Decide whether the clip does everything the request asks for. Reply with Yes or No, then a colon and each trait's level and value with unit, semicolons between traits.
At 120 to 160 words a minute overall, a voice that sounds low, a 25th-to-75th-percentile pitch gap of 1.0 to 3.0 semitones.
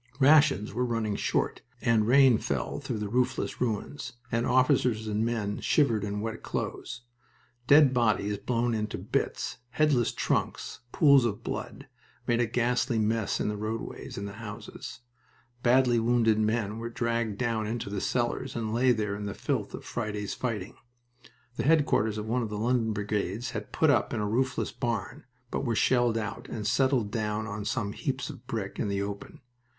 No: average, 175 wpm; low, 115 Hz; average, 2.7 semitones